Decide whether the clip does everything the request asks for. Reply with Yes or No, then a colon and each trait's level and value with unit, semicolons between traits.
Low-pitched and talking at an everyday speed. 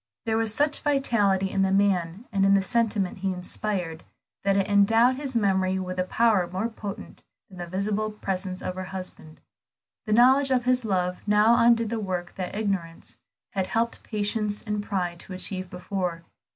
No: high, 200 Hz; average, 180 wpm